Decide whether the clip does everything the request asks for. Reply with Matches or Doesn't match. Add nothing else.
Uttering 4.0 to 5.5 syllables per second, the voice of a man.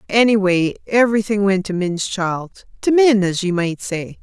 Doesn't match